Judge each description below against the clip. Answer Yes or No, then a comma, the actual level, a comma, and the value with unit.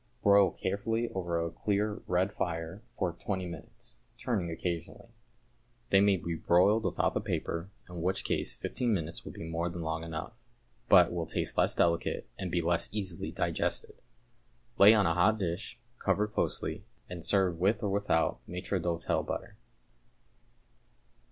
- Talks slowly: No, average, 155 wpm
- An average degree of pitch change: Yes, average, 3.3 semitones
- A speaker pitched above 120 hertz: No, very low, 90 Hz